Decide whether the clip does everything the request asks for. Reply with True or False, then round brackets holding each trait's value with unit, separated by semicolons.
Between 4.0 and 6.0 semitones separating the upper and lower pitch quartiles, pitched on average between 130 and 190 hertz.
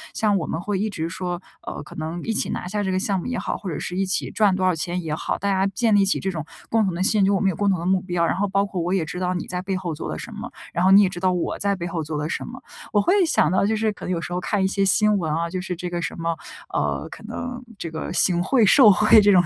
False (2.7 semitones; 185 Hz)